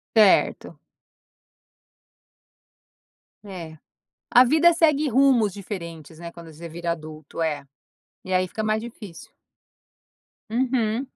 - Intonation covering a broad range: Yes, wide, 6.4 semitones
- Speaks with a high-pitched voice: Yes, high, 200 Hz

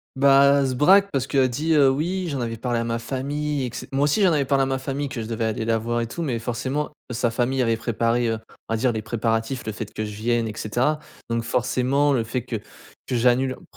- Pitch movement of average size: Yes, average, 3.3 semitones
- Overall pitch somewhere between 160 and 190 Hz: No, low, 125 Hz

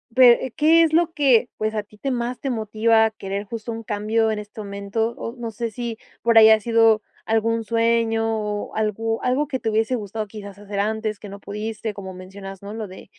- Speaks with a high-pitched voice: Yes, high, 220 Hz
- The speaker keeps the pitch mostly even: Yes, narrow, 1.8 semitones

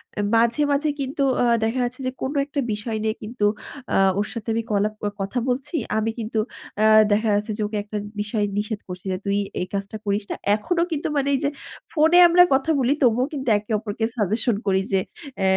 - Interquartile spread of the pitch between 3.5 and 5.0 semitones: Yes, average, 4.1 semitones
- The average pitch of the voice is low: No, high, 220 Hz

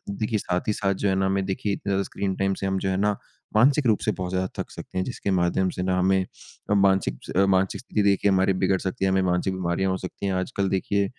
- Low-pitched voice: Yes, very low, 95 Hz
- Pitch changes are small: Yes, narrow, 1.1 semitones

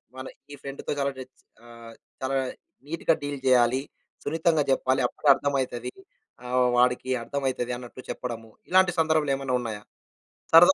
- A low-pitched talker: Yes, low, 130 Hz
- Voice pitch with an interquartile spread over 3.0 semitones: No, narrow, 2.5 semitones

